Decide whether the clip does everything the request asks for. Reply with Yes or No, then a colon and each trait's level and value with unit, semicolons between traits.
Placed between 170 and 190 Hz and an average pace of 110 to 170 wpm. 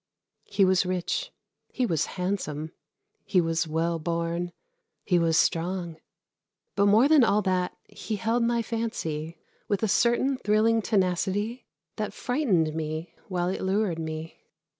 Yes: medium, 185 Hz; average, 140 wpm